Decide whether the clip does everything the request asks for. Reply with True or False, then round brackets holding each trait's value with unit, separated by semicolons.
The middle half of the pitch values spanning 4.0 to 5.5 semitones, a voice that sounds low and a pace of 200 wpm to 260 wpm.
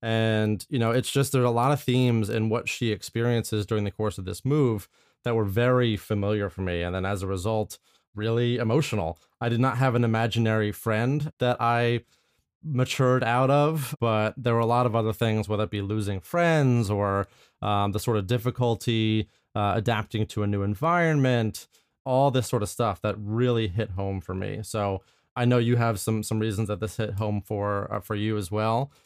False (2.7 semitones; 110 Hz; 205 wpm)